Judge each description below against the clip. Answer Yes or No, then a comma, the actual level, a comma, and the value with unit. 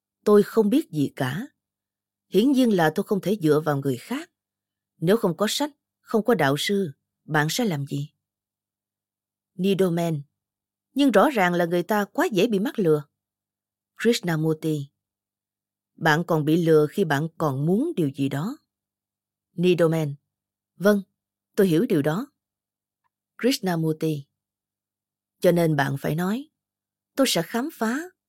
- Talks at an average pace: No, slow, 140 wpm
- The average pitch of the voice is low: No, medium, 155 Hz